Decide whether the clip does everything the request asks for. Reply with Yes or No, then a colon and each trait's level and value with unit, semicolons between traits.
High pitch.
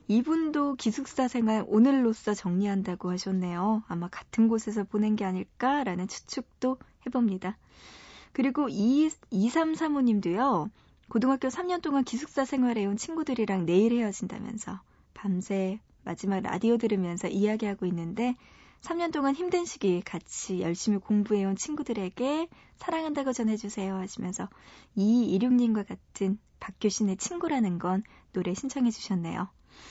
Yes: high, 220 Hz